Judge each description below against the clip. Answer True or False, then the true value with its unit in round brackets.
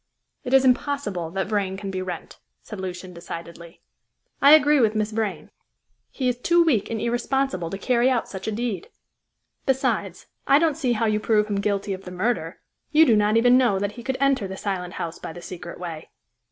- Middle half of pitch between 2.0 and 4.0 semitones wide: False (5.1 semitones)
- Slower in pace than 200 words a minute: False (205 wpm)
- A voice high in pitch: True (215 Hz)